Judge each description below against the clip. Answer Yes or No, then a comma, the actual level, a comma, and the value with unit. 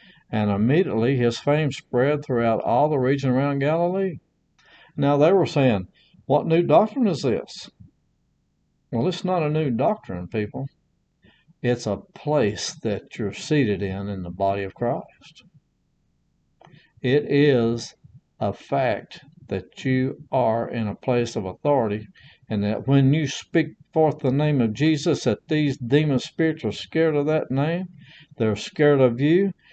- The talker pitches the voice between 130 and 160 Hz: Yes, medium, 140 Hz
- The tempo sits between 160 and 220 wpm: No, average, 150 wpm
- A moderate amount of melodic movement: Yes, average, 5.0 semitones